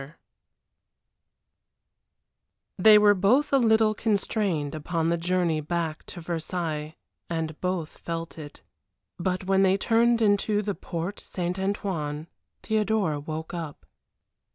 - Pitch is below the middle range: No, medium, 180 Hz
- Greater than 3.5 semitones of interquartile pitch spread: Yes, average, 4.3 semitones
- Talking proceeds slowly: Yes, slow, 120 wpm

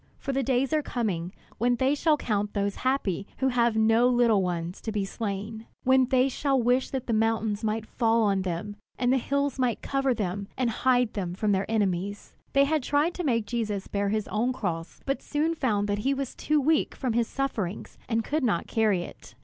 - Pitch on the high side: Yes, high, 230 Hz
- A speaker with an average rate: No, fast, 210 wpm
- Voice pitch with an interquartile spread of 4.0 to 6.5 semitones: Yes, average, 4.4 semitones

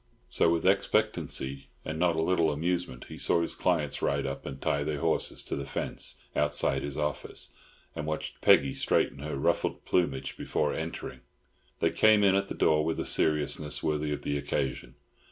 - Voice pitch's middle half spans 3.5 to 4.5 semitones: No, average, 3.0 semitones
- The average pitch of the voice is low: Yes, very low, 75 Hz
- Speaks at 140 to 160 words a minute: No, average, 180 wpm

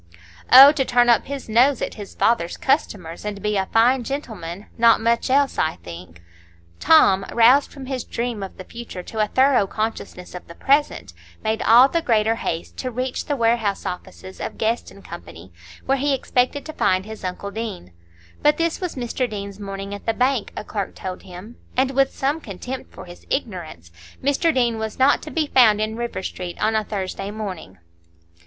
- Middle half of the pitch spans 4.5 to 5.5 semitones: Yes, average, 5.0 semitones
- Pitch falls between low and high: No, high, 225 Hz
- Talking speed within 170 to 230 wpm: Yes, average, 190 wpm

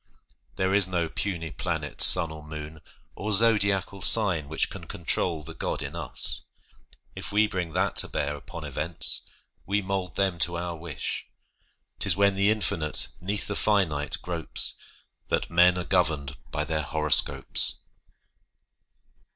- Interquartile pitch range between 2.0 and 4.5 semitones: Yes, average, 3.9 semitones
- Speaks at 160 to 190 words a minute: No, average, 145 wpm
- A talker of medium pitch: No, very low, 90 Hz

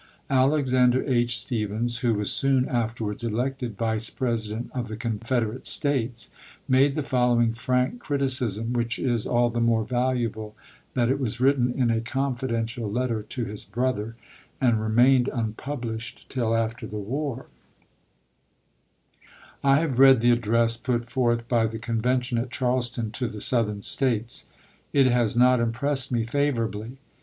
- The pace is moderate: Yes, average, 145 wpm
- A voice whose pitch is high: No, low, 120 Hz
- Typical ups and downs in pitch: No, narrow, 2.2 semitones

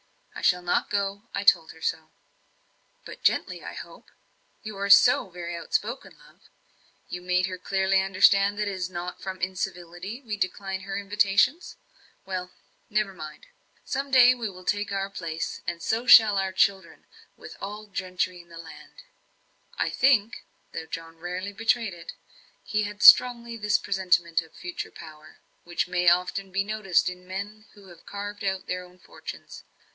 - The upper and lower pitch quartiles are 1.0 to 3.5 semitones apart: Yes, narrow, 2.5 semitones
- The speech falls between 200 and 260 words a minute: No, average, 165 wpm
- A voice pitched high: Yes, high, 195 Hz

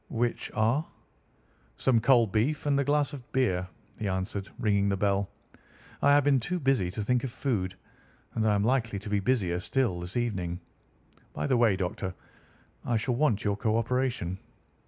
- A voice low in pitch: Yes, low, 110 Hz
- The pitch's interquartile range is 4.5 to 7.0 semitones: Yes, average, 4.9 semitones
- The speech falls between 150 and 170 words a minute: No, average, 180 wpm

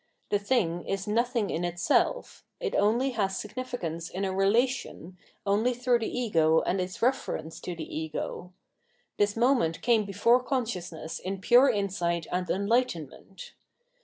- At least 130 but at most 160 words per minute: Yes, average, 140 wpm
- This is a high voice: Yes, high, 200 Hz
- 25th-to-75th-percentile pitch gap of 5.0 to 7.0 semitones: Yes, wide, 5.4 semitones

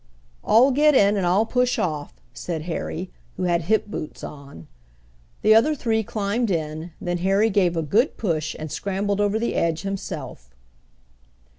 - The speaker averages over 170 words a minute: No, average, 160 wpm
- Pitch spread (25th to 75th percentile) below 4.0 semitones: No, average, 5.1 semitones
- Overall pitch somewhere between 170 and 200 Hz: Yes, high, 190 Hz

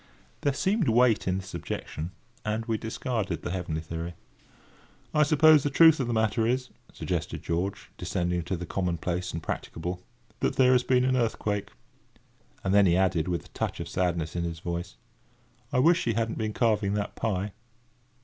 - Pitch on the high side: No, low, 100 Hz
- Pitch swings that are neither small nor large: No, wide, 6.0 semitones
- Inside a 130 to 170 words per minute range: No, average, 180 wpm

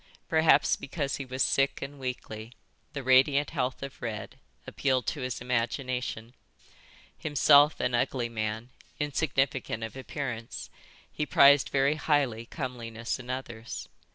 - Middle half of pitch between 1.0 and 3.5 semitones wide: Yes, average, 3.0 semitones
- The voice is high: No, low, 130 Hz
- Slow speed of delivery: Yes, slow, 125 wpm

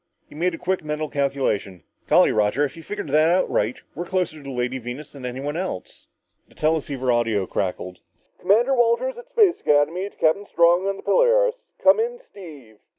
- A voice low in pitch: No, medium, 155 Hz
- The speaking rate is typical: Yes, average, 185 wpm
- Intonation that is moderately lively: No, wide, 7.1 semitones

